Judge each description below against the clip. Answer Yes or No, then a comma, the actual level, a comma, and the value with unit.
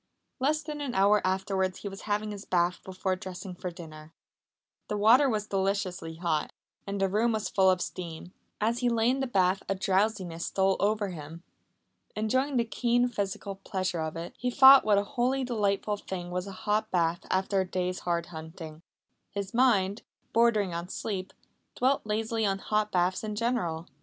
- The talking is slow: No, average, 180 wpm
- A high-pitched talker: Yes, high, 195 Hz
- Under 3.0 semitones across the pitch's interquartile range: No, average, 3.3 semitones